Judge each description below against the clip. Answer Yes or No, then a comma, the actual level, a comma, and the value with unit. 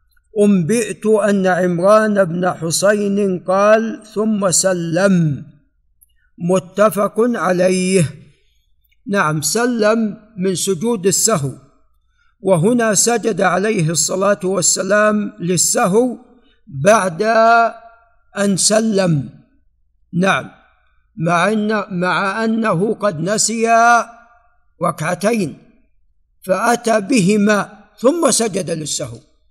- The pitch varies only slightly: No, average, 3.7 semitones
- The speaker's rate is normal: Yes, average, 75 wpm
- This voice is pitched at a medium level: No, high, 200 Hz